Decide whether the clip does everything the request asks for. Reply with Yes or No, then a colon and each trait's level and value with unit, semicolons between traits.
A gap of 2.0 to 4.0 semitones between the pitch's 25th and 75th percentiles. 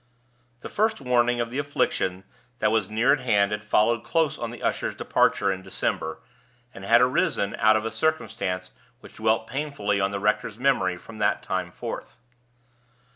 Yes: average, 3.6 semitones